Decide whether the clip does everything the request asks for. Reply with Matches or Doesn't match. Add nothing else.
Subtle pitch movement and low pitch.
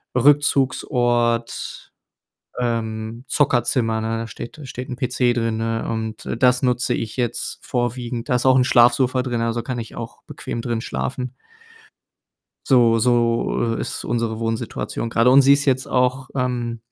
Matches